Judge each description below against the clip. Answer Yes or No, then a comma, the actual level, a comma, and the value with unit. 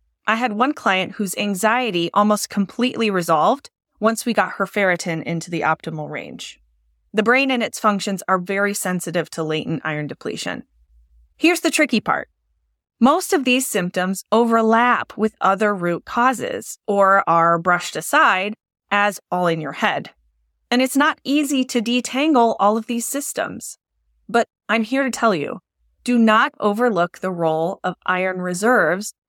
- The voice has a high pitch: Yes, high, 205 Hz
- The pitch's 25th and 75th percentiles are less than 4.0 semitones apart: No, average, 5.3 semitones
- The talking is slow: No, average, 155 wpm